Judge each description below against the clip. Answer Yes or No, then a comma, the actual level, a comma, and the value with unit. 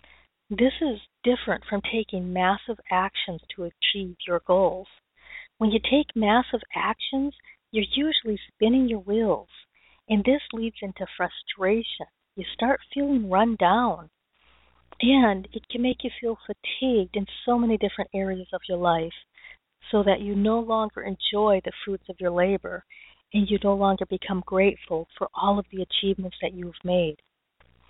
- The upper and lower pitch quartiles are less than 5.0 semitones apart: Yes, average, 3.5 semitones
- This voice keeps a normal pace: Yes, average, 155 wpm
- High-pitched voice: Yes, high, 200 Hz